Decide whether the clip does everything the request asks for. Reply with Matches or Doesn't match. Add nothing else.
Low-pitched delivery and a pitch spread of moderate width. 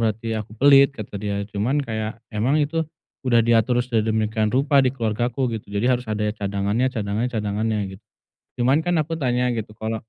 Matches